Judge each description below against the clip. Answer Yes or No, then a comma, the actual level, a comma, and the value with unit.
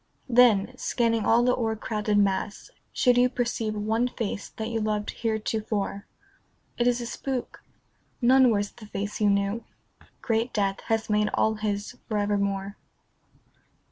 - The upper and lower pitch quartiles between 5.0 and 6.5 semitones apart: No, narrow, 2.5 semitones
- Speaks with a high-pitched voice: Yes, high, 220 Hz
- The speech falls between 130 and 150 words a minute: Yes, average, 140 wpm